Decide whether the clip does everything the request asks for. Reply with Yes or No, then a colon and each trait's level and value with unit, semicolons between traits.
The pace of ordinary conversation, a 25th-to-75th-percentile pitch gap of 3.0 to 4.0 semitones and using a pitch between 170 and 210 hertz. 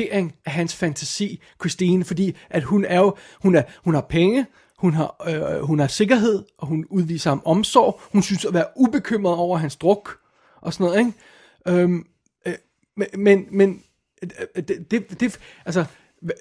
Yes: average, 170 wpm; average, 3.3 semitones; medium, 185 Hz